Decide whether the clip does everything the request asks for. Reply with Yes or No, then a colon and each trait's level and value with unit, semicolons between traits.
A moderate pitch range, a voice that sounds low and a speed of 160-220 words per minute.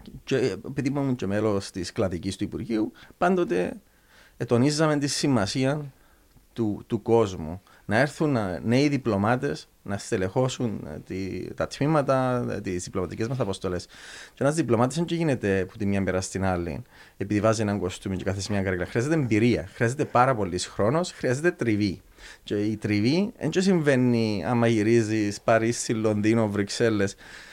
No: average, 4.9 semitones; low, 115 Hz; average, 145 wpm